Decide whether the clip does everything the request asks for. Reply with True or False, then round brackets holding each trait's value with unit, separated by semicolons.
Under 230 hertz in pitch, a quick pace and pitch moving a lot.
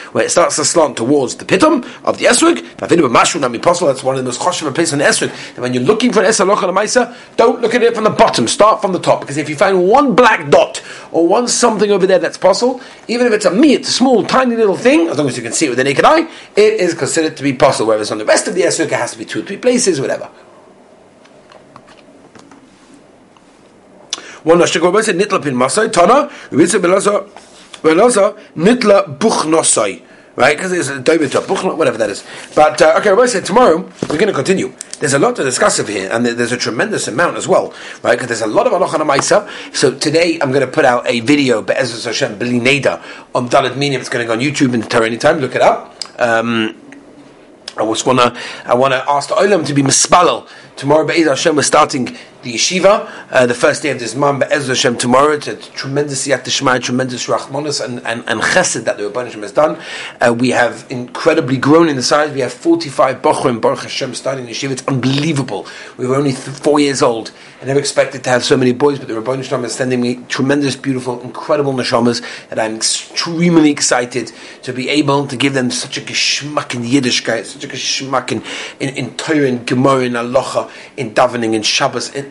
True (140 Hz; 215 wpm; 6.7 semitones)